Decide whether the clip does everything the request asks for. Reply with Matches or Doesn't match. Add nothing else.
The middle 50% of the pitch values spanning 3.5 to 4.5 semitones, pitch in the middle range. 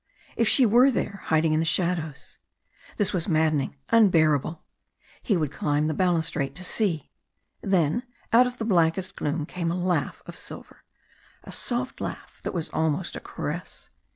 Matches